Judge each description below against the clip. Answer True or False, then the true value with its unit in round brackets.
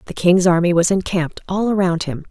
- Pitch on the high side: False (180 Hz)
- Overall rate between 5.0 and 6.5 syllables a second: True (5.9 syllables/s)